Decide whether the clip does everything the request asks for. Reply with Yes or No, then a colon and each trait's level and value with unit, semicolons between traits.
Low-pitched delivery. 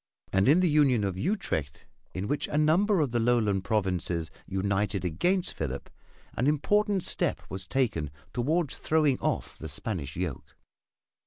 Yes: low, 115 Hz